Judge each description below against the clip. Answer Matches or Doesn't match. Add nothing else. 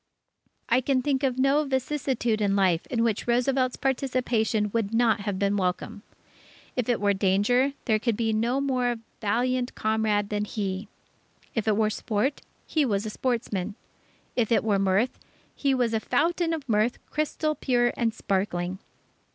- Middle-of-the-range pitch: Doesn't match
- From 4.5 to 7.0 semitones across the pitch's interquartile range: Doesn't match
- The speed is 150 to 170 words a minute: Matches